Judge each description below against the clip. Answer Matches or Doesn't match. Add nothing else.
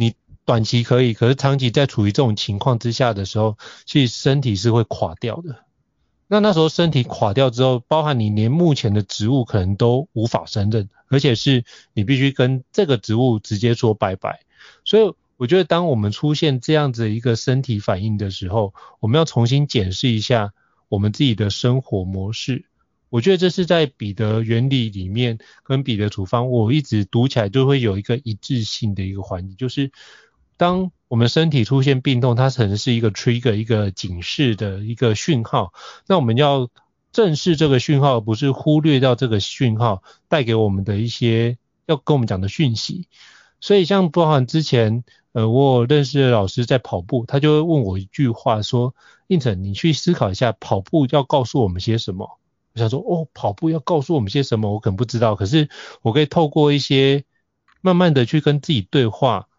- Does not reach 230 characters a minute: Doesn't match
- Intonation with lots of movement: Doesn't match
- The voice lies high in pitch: Doesn't match